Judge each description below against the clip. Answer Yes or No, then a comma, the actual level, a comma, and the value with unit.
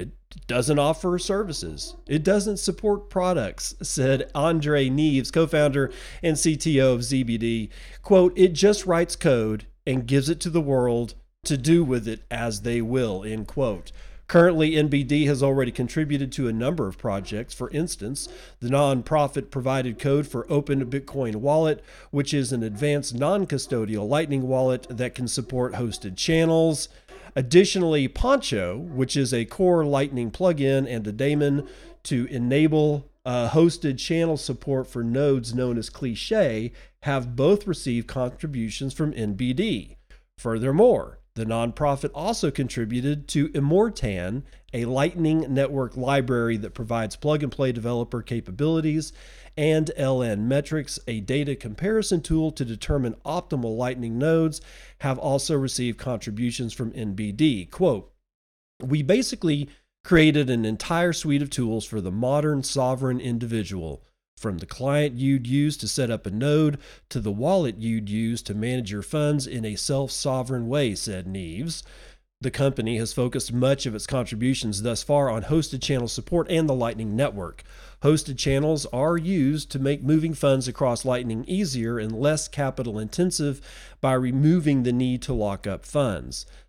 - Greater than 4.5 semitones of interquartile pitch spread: No, average, 4.2 semitones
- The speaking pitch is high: No, low, 135 Hz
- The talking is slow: No, average, 150 wpm